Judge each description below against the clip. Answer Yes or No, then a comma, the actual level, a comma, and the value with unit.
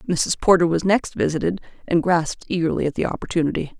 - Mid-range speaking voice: Yes, medium, 165 Hz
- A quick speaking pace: No, average, 175 wpm